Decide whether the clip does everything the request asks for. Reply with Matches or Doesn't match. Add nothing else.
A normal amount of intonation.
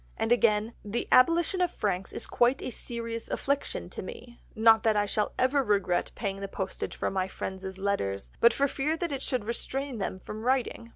Matches